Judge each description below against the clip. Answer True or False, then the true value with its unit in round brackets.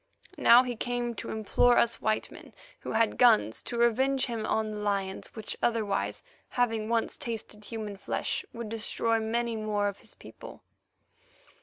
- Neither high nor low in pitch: False (225 Hz)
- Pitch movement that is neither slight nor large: False (2.0 semitones)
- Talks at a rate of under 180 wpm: True (160 wpm)